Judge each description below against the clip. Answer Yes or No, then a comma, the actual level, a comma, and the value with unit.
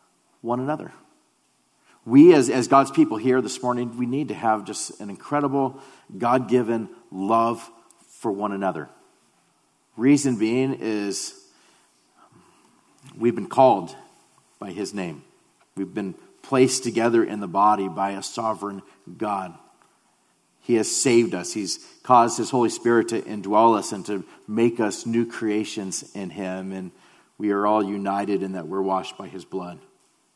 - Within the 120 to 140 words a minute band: No, average, 150 wpm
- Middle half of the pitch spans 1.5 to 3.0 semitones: No, average, 4.3 semitones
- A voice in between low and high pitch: No, low, 115 Hz